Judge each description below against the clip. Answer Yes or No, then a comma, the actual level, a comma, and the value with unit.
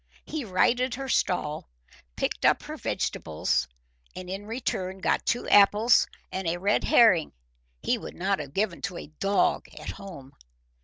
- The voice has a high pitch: Yes, high, 195 Hz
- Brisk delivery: No, average, 155 wpm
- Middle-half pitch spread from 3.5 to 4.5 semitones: Yes, average, 3.9 semitones